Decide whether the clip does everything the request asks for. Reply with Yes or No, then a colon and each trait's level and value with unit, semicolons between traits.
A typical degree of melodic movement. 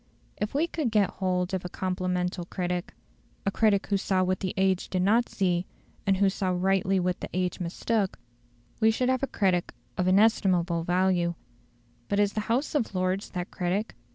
No: narrow, 2.2 semitones